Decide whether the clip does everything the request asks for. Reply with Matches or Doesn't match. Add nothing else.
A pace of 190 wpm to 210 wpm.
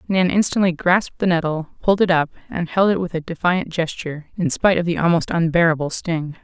Matches